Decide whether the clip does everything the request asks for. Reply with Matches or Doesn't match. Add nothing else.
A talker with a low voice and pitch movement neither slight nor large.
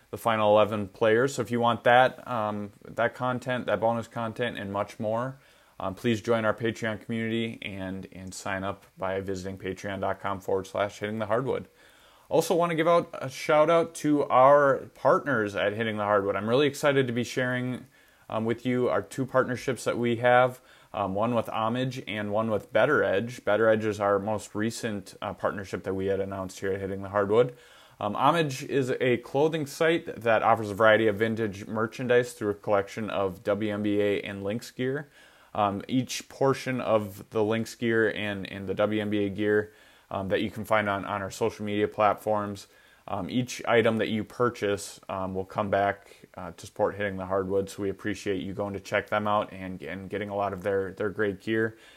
Matches